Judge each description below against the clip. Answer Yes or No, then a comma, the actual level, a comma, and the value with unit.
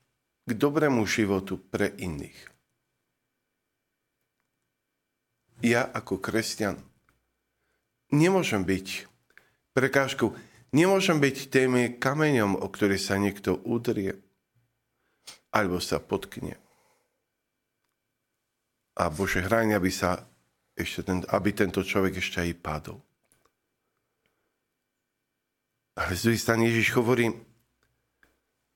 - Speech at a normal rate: No, slow, 85 wpm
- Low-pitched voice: Yes, low, 110 Hz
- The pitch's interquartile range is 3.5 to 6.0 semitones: Yes, average, 4.0 semitones